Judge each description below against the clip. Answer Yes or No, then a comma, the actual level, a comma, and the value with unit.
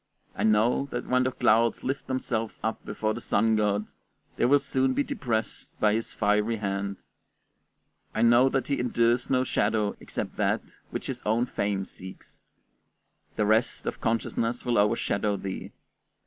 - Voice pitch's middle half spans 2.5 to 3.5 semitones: Yes, average, 2.8 semitones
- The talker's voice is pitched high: No, low, 115 Hz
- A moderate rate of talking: Yes, average, 160 wpm